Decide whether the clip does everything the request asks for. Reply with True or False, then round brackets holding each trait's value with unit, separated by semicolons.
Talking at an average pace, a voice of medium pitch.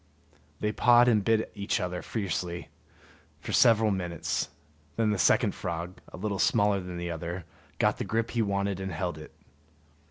False (165 wpm; 100 Hz)